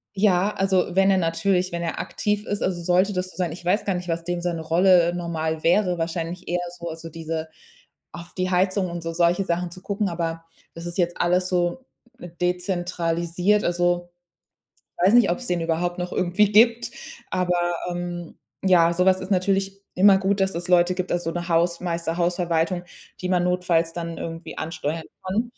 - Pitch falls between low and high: Yes, medium, 175 Hz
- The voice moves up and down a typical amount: No, narrow, 1.6 semitones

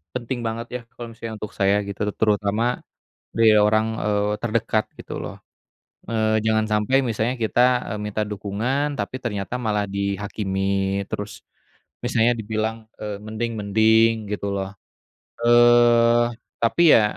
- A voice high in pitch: No, low, 110 Hz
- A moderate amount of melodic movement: No, narrow, 2.3 semitones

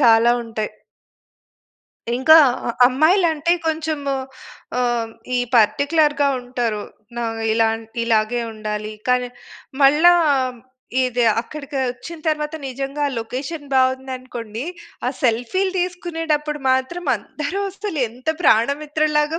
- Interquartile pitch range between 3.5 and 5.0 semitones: Yes, average, 4.6 semitones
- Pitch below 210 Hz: No, very high, 275 Hz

